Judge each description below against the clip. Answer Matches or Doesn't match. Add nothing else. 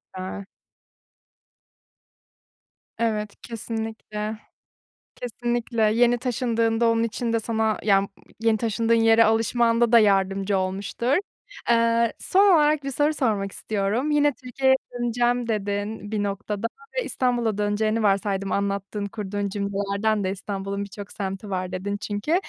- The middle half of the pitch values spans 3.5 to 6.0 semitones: Doesn't match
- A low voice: Doesn't match